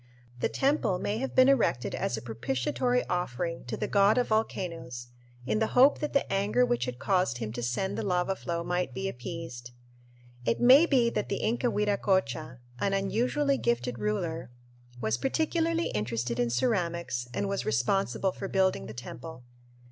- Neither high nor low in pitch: Yes, medium, 175 Hz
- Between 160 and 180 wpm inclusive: Yes, average, 170 wpm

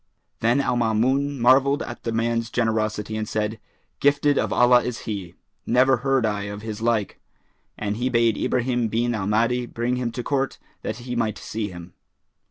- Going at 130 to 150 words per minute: No, average, 180 wpm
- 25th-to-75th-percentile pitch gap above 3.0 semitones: No, narrow, 2.4 semitones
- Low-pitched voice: Yes, low, 115 Hz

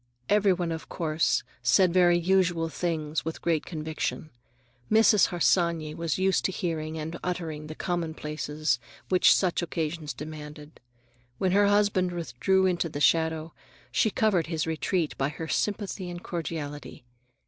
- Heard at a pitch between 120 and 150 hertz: No, medium, 165 Hz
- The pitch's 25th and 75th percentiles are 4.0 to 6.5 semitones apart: No, average, 2.7 semitones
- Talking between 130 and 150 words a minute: Yes, average, 140 wpm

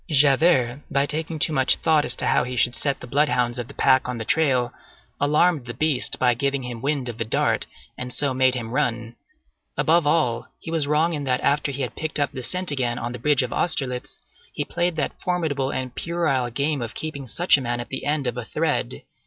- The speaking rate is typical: No, fast, 225 wpm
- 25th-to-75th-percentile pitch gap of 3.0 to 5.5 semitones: Yes, average, 3.6 semitones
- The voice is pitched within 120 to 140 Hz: Yes, low, 135 Hz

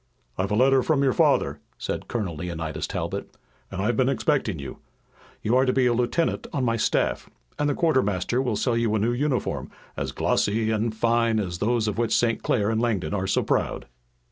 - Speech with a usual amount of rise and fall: Yes, average, 3.6 semitones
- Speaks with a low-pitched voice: Yes, low, 115 Hz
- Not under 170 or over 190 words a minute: No, fast, 205 wpm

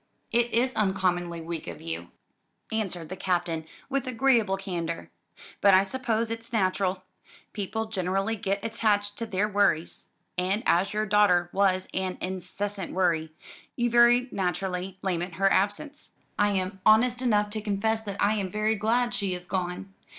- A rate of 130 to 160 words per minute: Yes, average, 155 wpm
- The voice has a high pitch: Yes, high, 200 Hz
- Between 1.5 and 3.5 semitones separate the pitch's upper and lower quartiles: Yes, average, 3.1 semitones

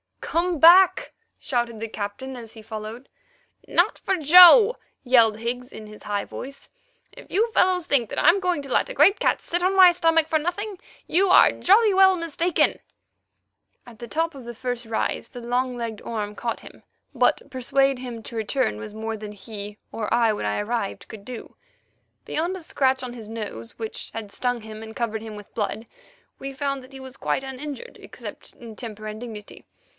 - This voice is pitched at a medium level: No, high, 245 Hz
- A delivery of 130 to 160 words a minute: No, average, 190 wpm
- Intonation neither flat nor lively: No, wide, 6.5 semitones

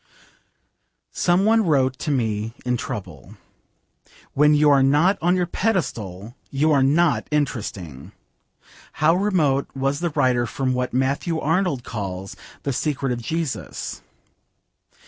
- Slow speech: Yes, slow, 125 wpm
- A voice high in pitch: No, medium, 140 Hz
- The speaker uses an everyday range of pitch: Yes, average, 5.0 semitones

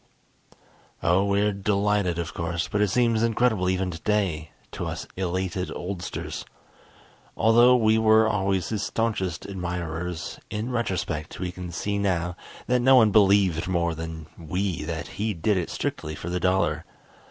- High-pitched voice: No, very low, 95 Hz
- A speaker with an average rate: Yes, average, 150 wpm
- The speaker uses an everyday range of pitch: Yes, average, 3.4 semitones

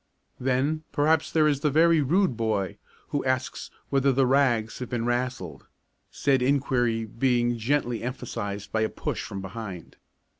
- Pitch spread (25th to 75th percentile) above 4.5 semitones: No, average, 3.8 semitones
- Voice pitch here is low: Yes, low, 125 Hz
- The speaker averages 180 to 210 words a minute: No, average, 150 wpm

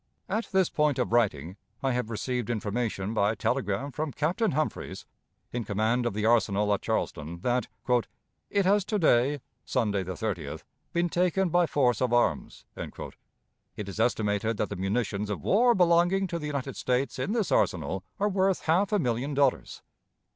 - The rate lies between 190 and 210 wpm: No, average, 170 wpm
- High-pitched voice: No, low, 125 Hz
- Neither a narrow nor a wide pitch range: No, wide, 8.3 semitones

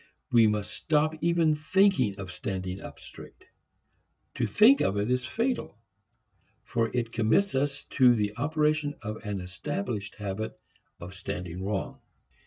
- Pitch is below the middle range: Yes, low, 115 Hz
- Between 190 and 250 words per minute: No, average, 140 wpm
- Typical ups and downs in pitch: No, wide, 7.2 semitones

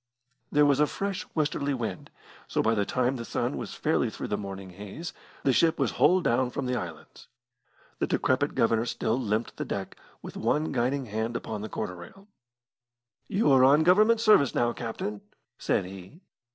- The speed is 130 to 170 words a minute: No, average, 180 wpm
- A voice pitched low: Yes, low, 125 Hz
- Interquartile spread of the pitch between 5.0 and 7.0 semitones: Yes, wide, 5.6 semitones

